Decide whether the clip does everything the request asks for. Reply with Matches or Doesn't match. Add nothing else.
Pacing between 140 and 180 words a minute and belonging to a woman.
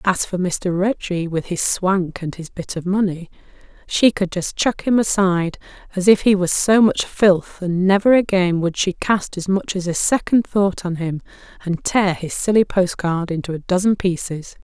Doesn't match